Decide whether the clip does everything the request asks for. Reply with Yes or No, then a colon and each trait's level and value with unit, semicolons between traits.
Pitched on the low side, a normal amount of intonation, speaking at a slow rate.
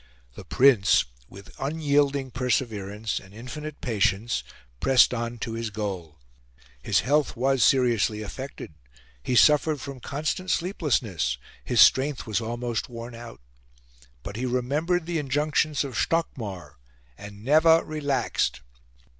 Yes: low, 125 Hz; average, 5.0 semitones; slow, 120 wpm